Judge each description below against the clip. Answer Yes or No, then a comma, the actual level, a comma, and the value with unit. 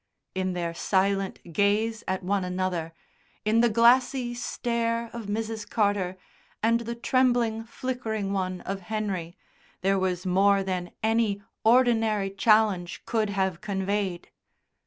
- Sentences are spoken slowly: Yes, slow, 125 wpm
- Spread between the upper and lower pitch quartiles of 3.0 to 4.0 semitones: Yes, average, 3.3 semitones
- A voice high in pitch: Yes, high, 205 Hz